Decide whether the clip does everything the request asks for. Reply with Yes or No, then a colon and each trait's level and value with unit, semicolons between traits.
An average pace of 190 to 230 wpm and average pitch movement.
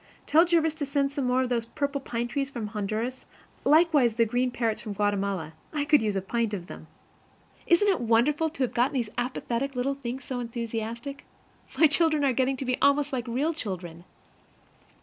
Yes: average, 195 wpm; average, 3.7 semitones